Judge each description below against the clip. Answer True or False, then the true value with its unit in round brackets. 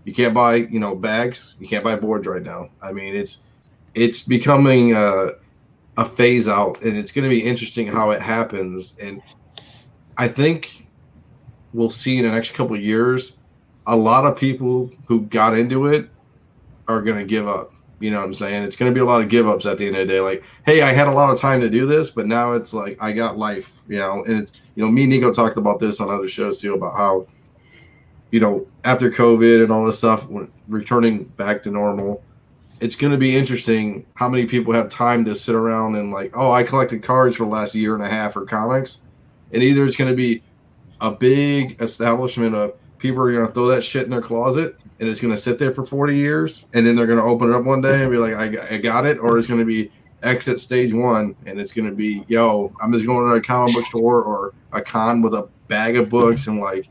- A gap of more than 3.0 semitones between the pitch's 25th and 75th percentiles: False (2.7 semitones)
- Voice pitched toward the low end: True (115 Hz)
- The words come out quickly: True (235 wpm)